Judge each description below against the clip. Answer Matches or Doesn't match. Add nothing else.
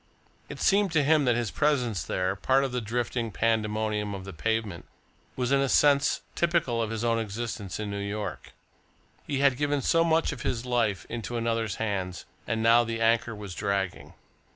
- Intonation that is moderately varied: Matches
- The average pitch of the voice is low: Matches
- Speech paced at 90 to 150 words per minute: Doesn't match